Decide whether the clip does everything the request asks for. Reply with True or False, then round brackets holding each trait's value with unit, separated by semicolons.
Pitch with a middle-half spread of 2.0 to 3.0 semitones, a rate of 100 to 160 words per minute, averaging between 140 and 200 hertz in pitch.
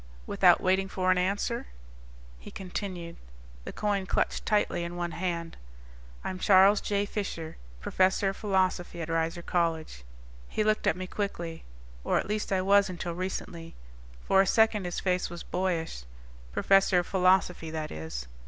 True (2.5 semitones; 155 wpm; 185 Hz)